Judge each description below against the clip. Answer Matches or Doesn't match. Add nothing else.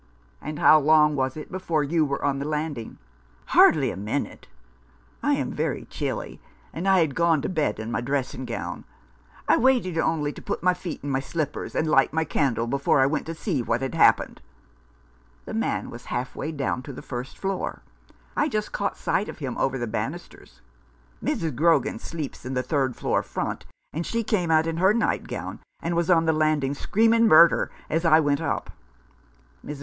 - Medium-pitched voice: Matches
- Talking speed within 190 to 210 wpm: Matches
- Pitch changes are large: Doesn't match